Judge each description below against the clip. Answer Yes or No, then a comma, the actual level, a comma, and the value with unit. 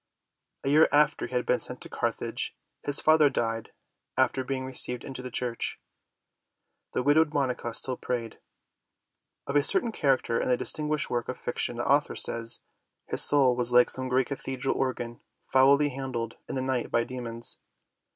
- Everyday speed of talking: Yes, average, 170 wpm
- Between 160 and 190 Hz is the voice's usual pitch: No, low, 130 Hz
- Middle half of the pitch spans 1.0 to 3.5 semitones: Yes, narrow, 2.4 semitones